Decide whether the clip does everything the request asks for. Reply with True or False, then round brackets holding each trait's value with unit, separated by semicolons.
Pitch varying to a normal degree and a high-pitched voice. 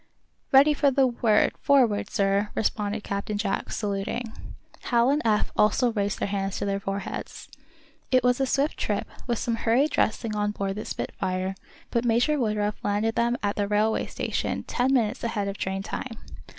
True (3.3 semitones; 215 Hz)